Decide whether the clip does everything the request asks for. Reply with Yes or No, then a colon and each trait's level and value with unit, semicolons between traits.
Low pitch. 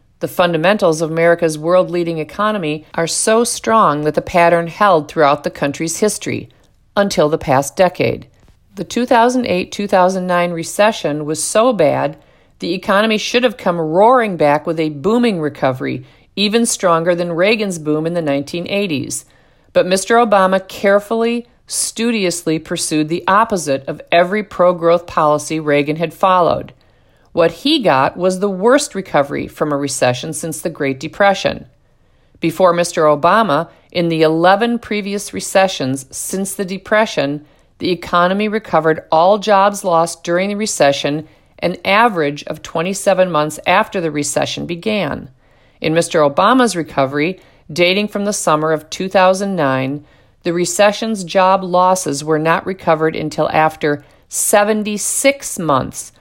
No: medium, 175 Hz